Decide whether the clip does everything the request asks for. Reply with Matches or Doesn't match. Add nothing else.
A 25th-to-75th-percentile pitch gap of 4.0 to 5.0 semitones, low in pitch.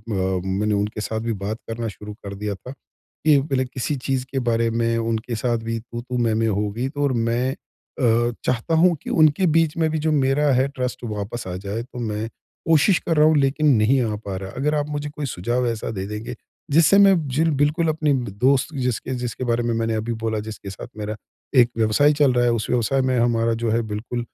Matches